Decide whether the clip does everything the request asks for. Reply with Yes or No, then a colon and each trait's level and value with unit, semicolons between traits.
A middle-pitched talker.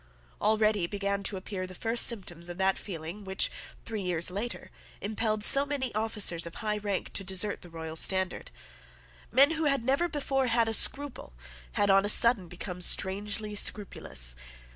No: high, 205 Hz